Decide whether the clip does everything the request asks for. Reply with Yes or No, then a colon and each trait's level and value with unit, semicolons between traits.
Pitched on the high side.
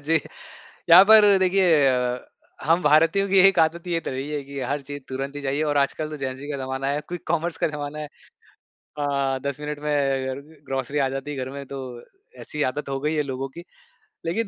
No: medium, 145 Hz